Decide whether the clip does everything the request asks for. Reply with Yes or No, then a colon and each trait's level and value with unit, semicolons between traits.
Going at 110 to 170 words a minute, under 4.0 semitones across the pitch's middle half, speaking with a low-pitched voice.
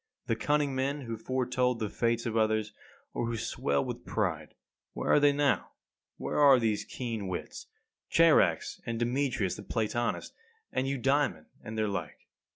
Yes: average, 160 wpm; average, 3.5 semitones; low, 120 Hz